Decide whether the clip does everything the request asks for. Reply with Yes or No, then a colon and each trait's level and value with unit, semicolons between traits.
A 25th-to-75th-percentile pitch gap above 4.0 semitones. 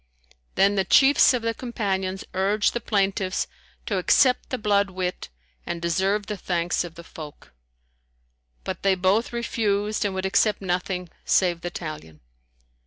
No: average, 2.7 semitones